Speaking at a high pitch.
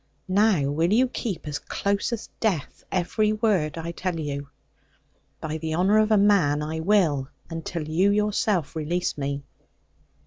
No: medium, 175 Hz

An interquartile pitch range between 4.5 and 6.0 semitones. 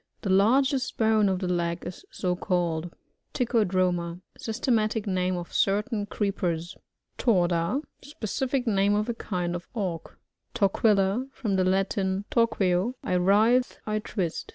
No: average, 3.7 semitones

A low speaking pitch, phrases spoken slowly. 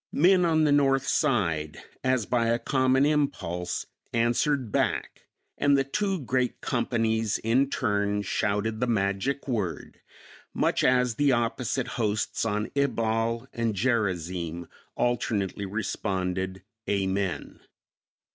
Yes: low, 115 Hz; slow, 115 wpm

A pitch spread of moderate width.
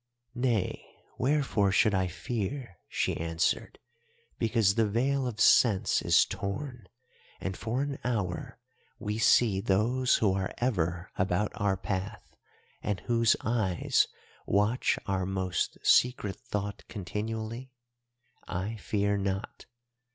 Yes: average, 3.8 semitones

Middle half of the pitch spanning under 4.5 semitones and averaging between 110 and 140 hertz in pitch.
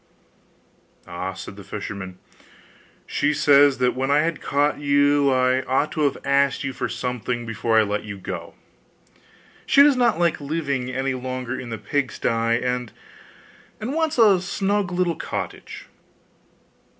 Yes: average, 3.9 semitones; low, 135 Hz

